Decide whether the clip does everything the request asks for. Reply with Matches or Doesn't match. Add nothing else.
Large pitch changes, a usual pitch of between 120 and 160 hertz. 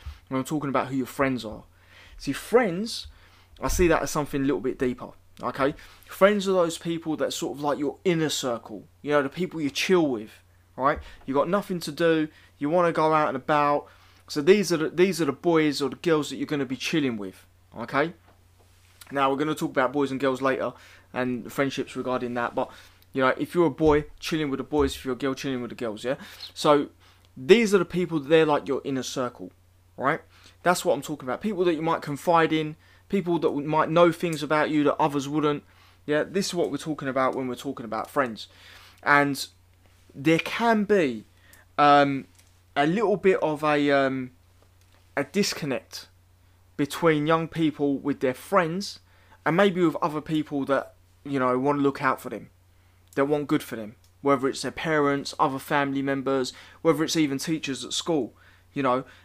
Matches